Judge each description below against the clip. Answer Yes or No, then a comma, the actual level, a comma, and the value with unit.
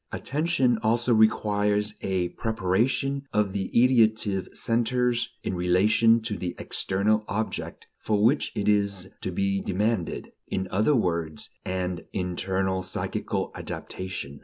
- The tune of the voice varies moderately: Yes, average, 3.4 semitones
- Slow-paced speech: Yes, slow, 120 wpm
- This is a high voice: No, low, 105 Hz